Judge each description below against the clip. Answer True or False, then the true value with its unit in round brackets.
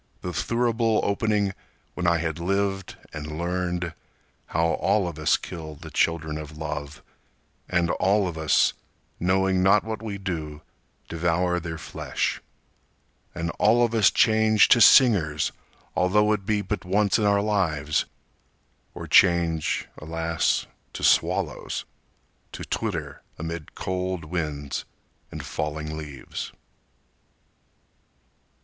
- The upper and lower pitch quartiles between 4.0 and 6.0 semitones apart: True (4.3 semitones)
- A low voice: True (90 Hz)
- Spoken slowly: True (115 wpm)